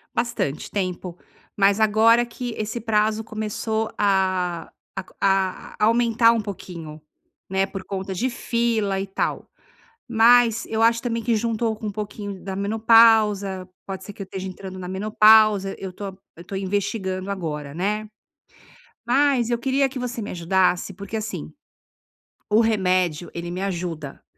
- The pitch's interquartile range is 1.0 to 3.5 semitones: Yes, average, 3.1 semitones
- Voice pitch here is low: No, high, 205 Hz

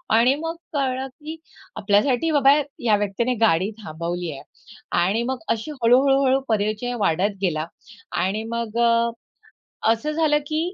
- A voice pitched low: No, high, 235 Hz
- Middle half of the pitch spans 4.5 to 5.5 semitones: Yes, average, 4.9 semitones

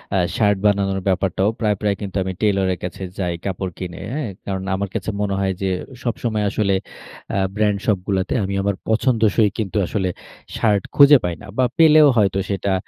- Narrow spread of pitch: Yes, narrow, 2.1 semitones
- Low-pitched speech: Yes, low, 100 Hz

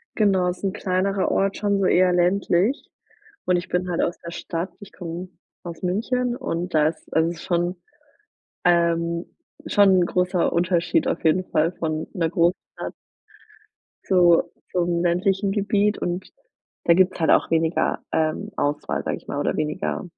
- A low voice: No, medium, 180 Hz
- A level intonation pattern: Yes, narrow, 2.2 semitones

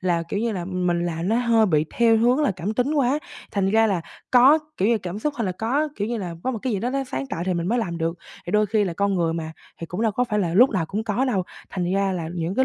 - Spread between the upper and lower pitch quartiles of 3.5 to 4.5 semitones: No, average, 5.2 semitones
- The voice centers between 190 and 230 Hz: Yes, high, 200 Hz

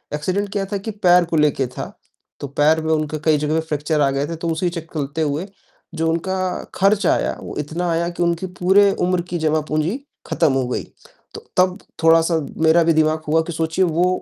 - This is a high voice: No, medium, 165 Hz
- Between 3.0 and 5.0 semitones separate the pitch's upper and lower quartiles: No, narrow, 2.6 semitones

